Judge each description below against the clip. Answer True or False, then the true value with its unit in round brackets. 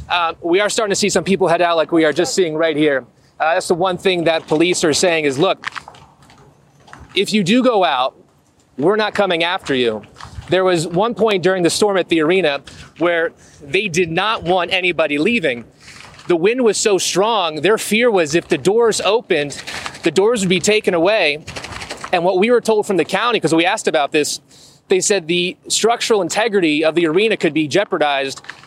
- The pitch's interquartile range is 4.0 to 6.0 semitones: True (4.5 semitones)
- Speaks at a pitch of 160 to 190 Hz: True (185 Hz)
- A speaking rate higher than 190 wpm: True (205 wpm)